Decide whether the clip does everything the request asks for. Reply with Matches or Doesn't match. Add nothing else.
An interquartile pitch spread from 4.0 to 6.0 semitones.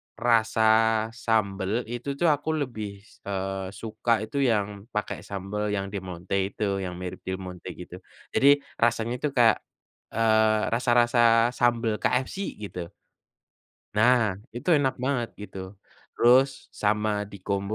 Doesn't match